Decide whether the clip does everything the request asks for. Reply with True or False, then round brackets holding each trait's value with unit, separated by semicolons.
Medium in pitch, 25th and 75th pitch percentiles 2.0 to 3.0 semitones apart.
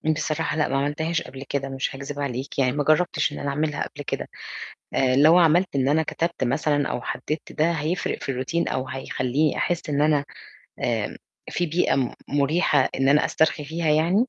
True (145 Hz; 2.7 semitones)